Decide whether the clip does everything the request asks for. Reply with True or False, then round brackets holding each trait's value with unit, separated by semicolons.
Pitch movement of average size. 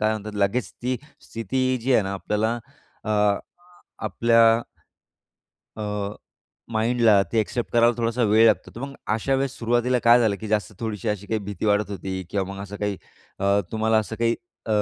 False (2.3 semitones)